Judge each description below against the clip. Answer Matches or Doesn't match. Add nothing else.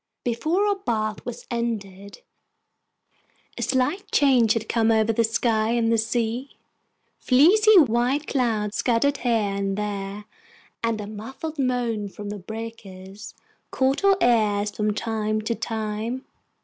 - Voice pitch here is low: Doesn't match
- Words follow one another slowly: Matches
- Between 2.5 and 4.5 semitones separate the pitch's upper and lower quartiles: Matches